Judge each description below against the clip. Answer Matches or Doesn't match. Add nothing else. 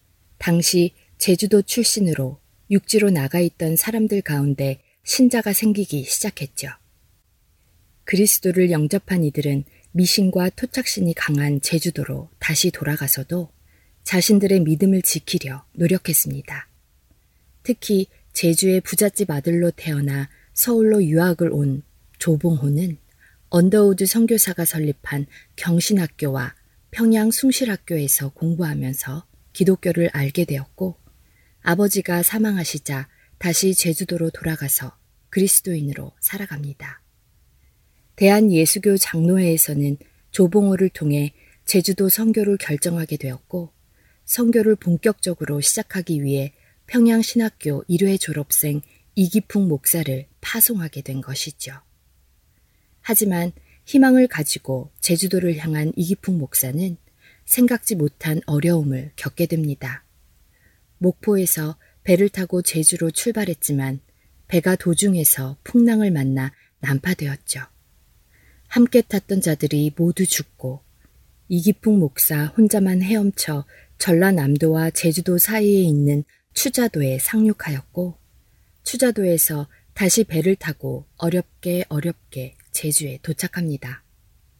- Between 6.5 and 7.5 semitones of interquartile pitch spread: Doesn't match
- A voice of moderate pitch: Matches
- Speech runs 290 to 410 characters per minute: Doesn't match